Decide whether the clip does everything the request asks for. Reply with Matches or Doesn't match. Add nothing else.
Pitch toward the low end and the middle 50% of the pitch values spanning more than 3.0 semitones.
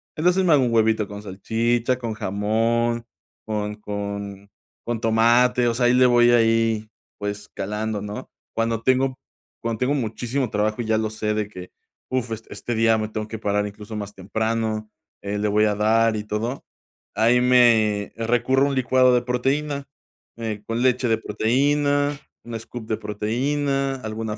Doesn't match